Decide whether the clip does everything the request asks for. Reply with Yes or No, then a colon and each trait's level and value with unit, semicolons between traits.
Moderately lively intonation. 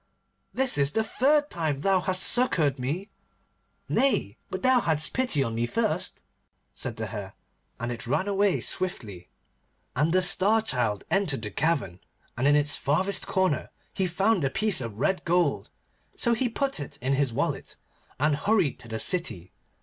No: wide, 7.5 semitones